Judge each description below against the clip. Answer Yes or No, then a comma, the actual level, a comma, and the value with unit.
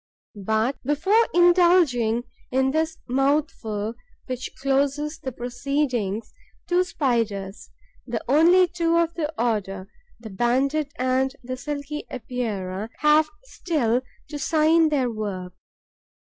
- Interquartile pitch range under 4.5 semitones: No, average, 5.1 semitones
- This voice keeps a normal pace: No, slow, 110 wpm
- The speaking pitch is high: Yes, very high, 265 Hz